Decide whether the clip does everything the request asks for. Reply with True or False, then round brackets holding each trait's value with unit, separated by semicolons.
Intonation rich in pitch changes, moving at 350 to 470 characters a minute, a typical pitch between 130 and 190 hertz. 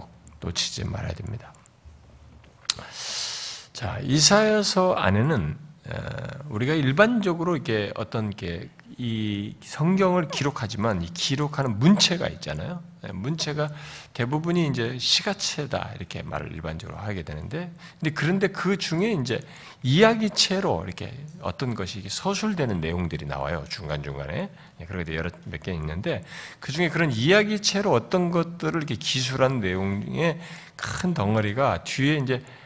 False (8.8 semitones; 295 characters per minute; 140 Hz)